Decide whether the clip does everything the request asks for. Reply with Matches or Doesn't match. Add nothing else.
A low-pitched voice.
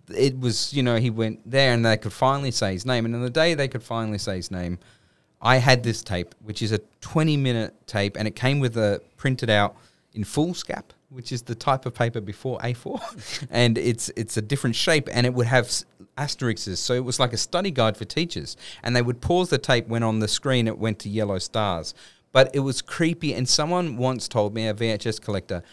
Matches